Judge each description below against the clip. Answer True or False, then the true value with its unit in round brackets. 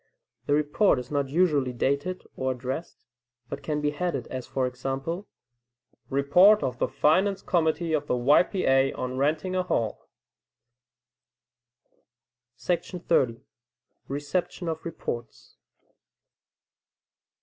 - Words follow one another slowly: True (115 wpm)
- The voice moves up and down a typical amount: True (4.8 semitones)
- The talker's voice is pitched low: False (145 Hz)